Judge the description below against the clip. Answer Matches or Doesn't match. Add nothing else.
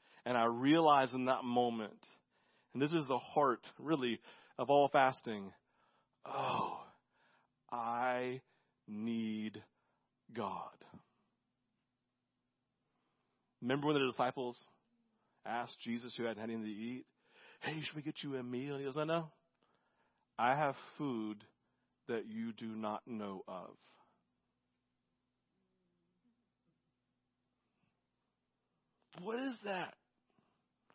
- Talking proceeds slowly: Matches